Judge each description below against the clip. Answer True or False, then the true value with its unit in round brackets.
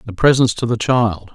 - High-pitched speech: False (115 Hz)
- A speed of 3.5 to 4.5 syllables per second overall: False (5.0 syllables/s)